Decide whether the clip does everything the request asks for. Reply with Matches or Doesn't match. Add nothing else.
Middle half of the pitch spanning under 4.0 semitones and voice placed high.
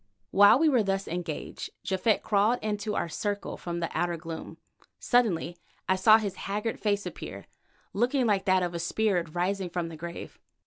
Matches